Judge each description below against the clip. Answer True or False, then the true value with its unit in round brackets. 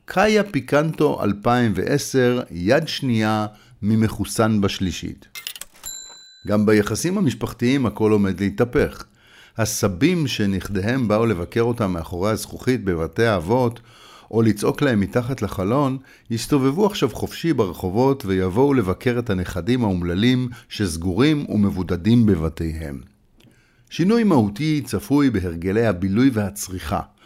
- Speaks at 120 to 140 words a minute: False (100 wpm)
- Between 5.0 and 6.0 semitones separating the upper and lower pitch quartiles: False (4.5 semitones)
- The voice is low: True (110 Hz)